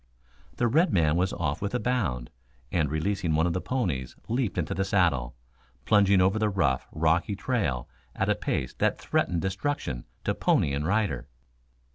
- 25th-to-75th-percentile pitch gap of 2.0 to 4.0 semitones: No, average, 5.2 semitones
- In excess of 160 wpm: Yes, average, 170 wpm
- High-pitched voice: No, very low, 90 Hz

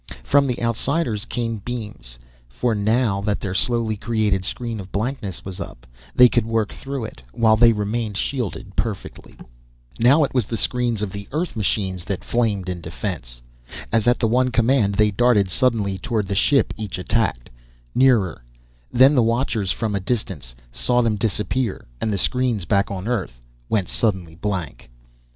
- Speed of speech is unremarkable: Yes, average, 170 wpm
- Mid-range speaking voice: No, low, 110 Hz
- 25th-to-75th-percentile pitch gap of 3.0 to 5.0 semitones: Yes, average, 3.8 semitones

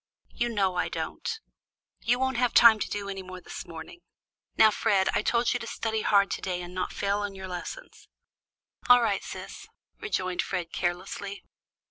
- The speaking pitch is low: No, high, 200 Hz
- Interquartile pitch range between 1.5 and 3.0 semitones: No, average, 4.0 semitones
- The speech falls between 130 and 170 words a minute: No, average, 180 wpm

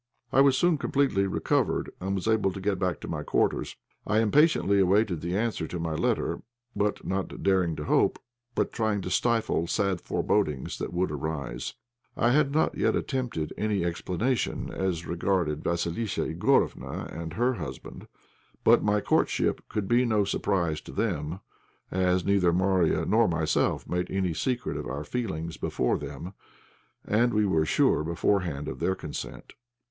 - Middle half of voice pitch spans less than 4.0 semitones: No, average, 4.4 semitones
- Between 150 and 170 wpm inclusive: Yes, average, 160 wpm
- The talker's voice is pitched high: No, very low, 95 Hz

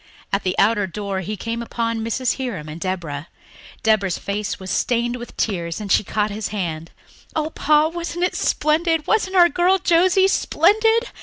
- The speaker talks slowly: No, average, 175 wpm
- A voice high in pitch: Yes, high, 230 Hz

